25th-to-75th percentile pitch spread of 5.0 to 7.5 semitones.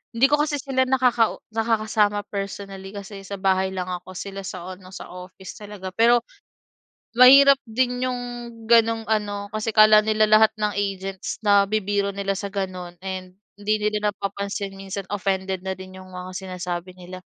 No: narrow, 2.4 semitones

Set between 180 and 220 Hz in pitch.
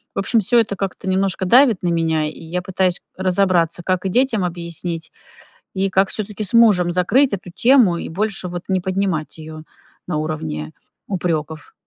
Yes: medium, 185 Hz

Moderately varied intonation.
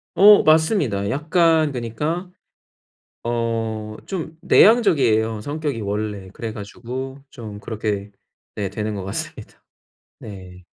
No: wide, 7.0 semitones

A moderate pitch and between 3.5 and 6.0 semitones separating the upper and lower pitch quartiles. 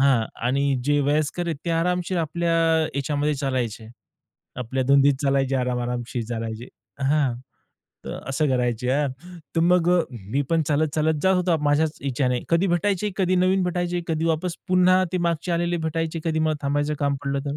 Yes: medium, 150 Hz; average, 4.1 semitones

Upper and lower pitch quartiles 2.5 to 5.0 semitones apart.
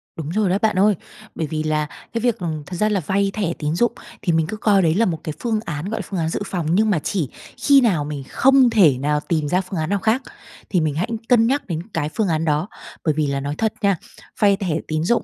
No: wide, 5.4 semitones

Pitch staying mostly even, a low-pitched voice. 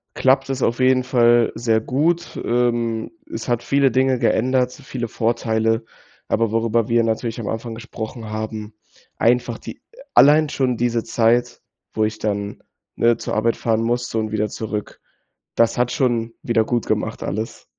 Yes: narrow, 1.8 semitones; low, 115 Hz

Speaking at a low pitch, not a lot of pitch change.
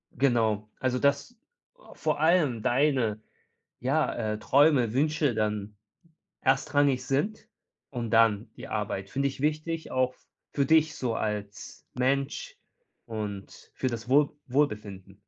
No: low, 130 Hz; average, 5.0 semitones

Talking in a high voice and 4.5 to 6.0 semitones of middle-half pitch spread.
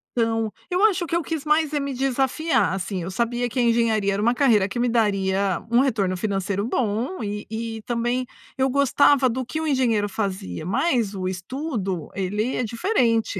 Yes: high, 230 Hz; average, 4.8 semitones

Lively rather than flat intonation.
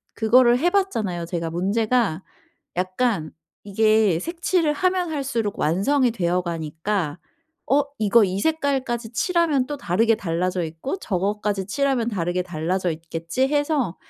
Yes: wide, 7.2 semitones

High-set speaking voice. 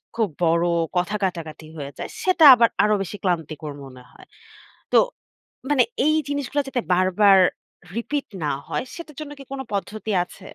Yes: high, 205 Hz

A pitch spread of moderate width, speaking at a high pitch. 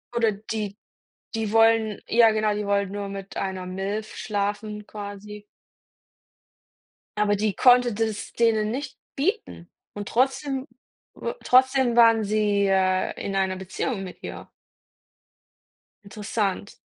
No: narrow, 2.2 semitones; high, 210 Hz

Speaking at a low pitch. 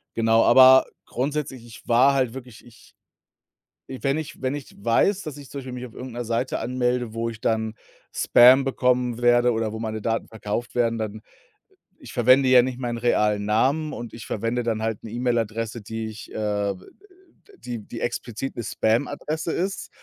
Yes: low, 120 Hz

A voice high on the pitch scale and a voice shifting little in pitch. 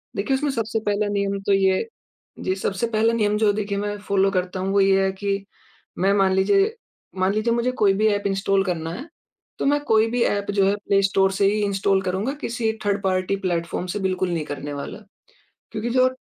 Yes: high, 200 Hz; narrow, 2.1 semitones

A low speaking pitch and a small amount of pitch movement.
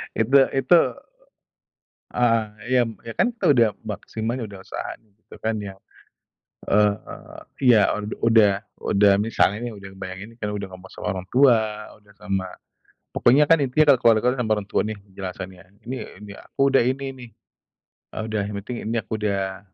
No: low, 110 Hz; average, 3.3 semitones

